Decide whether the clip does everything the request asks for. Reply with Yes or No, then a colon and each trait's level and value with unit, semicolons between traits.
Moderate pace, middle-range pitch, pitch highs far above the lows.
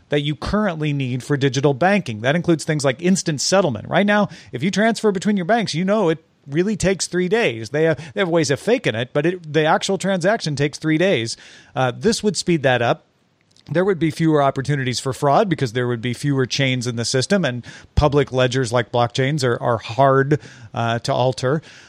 No: fast, 210 wpm; medium, 145 Hz; wide, 5.7 semitones